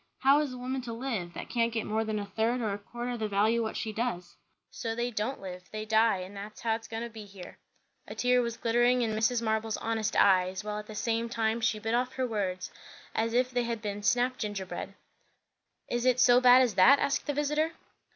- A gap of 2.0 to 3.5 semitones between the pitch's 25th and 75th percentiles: Yes, average, 2.7 semitones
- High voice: Yes, high, 225 Hz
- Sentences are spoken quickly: Yes, fast, 235 wpm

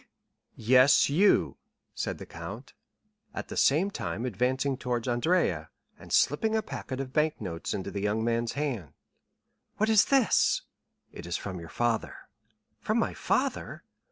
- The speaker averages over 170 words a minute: No, average, 150 wpm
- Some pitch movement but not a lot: No, wide, 6.4 semitones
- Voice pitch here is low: Yes, low, 125 Hz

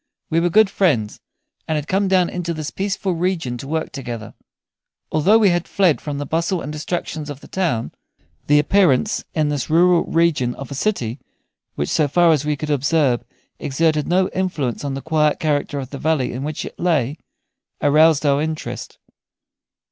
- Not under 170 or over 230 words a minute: Yes, average, 180 wpm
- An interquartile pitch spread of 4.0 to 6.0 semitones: No, average, 3.6 semitones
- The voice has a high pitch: No, medium, 155 Hz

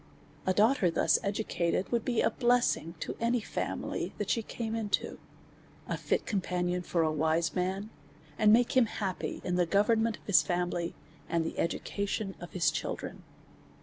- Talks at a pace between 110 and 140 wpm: No, average, 165 wpm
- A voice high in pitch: Yes, high, 195 Hz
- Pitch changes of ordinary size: Yes, average, 4.2 semitones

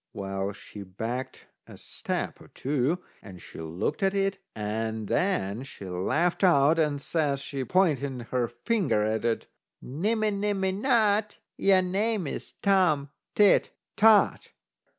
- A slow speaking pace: Yes, slow, 130 wpm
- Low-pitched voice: No, medium, 145 Hz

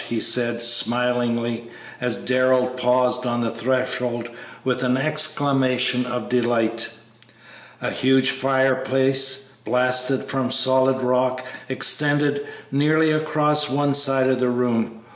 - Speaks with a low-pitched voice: Yes, low, 130 Hz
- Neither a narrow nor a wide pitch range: No, narrow, 1.6 semitones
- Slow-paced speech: Yes, slow, 120 wpm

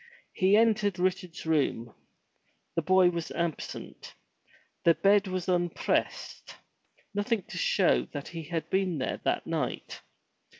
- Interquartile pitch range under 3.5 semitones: Yes, average, 2.8 semitones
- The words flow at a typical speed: No, slow, 125 wpm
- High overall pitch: No, medium, 180 Hz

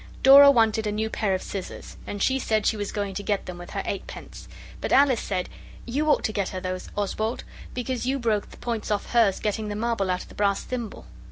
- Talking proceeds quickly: Yes, fast, 250 wpm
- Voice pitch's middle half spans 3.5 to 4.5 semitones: No, average, 3.1 semitones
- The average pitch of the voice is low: No, high, 215 Hz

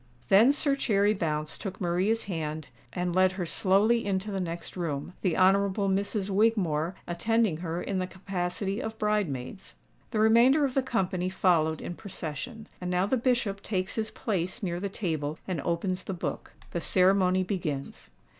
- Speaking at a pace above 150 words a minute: Yes, average, 165 wpm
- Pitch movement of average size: Yes, average, 3.4 semitones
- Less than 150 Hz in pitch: No, high, 190 Hz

